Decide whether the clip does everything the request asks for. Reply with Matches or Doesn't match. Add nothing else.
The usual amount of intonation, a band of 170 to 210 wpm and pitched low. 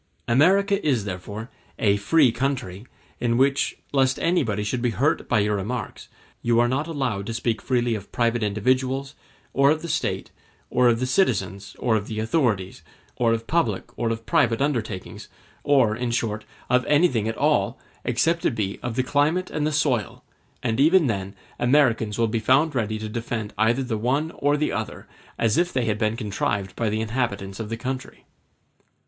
Matches